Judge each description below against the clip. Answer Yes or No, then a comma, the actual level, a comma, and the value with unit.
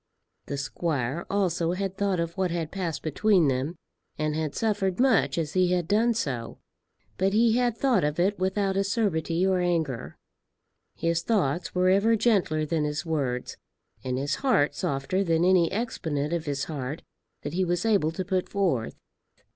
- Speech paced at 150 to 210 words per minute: Yes, average, 170 wpm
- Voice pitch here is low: No, medium, 175 Hz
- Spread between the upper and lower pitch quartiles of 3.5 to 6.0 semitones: Yes, average, 4.4 semitones